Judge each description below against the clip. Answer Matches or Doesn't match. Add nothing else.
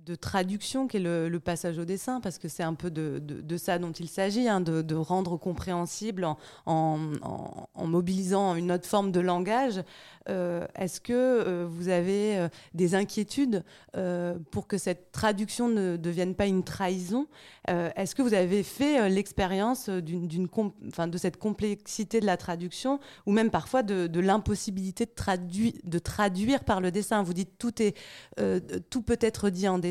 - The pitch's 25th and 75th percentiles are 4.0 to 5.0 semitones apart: Doesn't match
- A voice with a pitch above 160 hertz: Matches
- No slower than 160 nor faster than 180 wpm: Doesn't match